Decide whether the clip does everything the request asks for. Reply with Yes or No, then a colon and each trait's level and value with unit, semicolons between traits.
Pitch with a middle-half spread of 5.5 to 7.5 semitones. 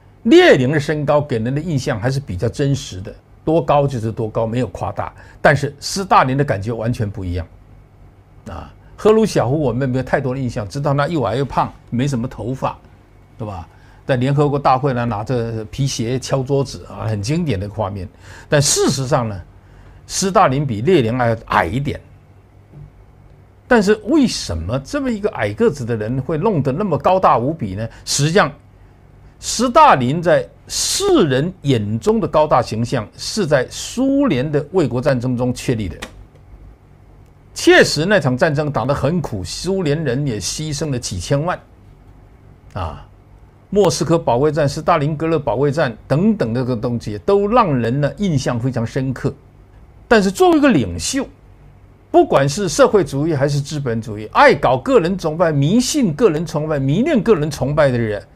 Yes: wide, 5.8 semitones